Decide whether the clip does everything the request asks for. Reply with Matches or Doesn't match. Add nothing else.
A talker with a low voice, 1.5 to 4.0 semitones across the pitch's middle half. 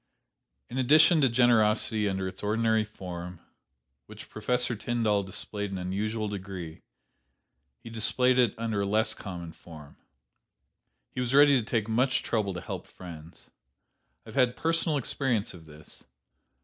Doesn't match